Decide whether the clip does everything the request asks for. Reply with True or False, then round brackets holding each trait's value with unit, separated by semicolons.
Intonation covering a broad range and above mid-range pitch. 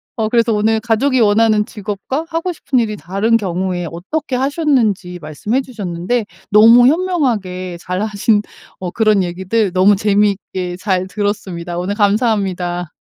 False (3.8 semitones; 210 Hz)